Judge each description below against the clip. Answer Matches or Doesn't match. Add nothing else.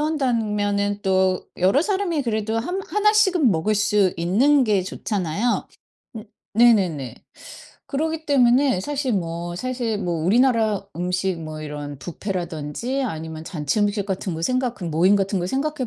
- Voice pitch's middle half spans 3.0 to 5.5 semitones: Doesn't match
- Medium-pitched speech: Doesn't match